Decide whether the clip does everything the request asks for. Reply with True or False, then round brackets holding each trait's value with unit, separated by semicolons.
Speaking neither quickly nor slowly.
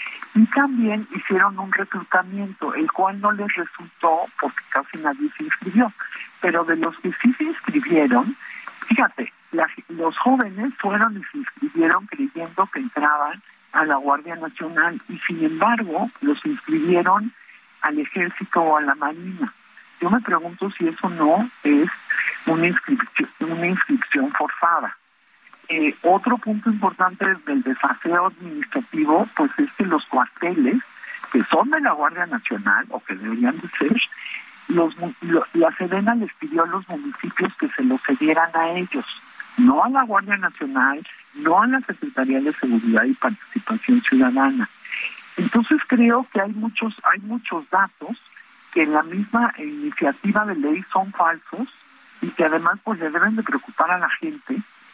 True (155 wpm)